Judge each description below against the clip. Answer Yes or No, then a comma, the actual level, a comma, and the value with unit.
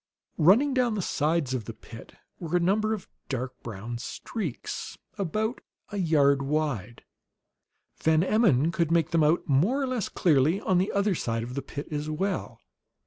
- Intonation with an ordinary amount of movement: No, wide, 6.2 semitones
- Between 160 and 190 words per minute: Yes, average, 170 wpm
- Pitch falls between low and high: Yes, medium, 165 Hz